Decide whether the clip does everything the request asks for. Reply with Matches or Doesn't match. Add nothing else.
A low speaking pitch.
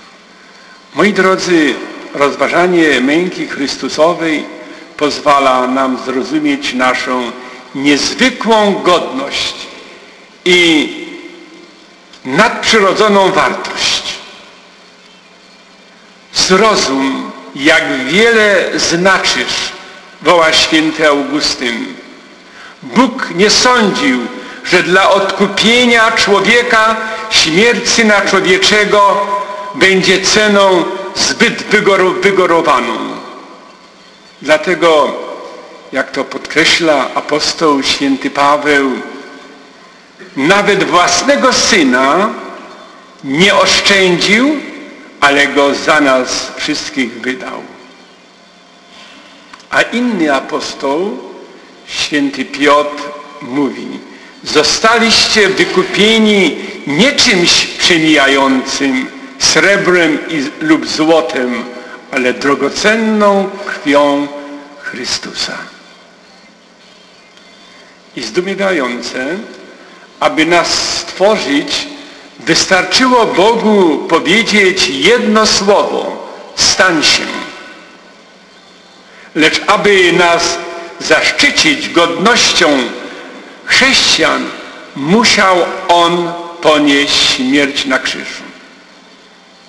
Doesn't match